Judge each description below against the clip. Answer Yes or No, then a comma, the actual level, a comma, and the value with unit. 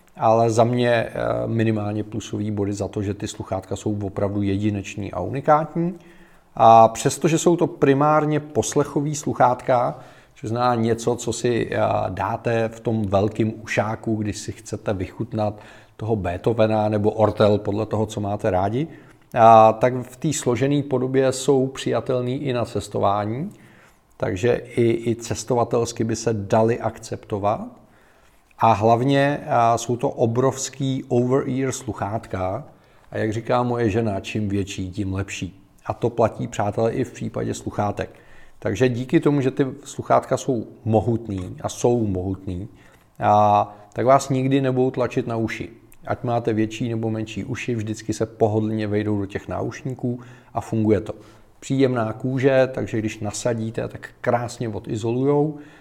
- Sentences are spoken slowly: No, average, 140 wpm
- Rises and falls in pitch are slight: No, average, 3.2 semitones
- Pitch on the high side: No, low, 115 Hz